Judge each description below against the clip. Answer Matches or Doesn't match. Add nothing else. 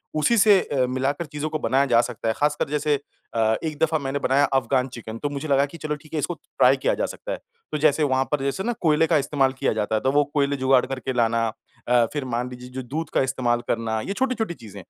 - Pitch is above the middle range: Doesn't match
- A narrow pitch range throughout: Doesn't match